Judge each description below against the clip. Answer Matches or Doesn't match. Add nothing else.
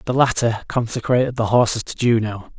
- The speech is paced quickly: Doesn't match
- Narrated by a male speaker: Matches